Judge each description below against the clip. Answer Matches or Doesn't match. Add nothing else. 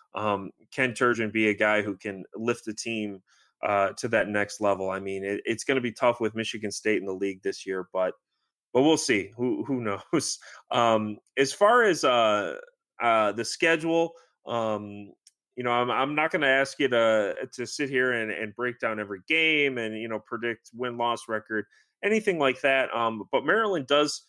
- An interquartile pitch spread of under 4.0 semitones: Doesn't match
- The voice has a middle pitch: Doesn't match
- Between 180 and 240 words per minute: Matches